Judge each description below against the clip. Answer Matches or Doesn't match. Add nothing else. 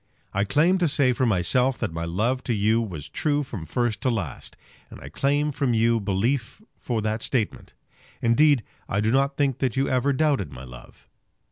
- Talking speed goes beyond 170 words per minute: Matches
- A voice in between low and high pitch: Doesn't match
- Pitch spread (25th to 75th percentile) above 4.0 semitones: Matches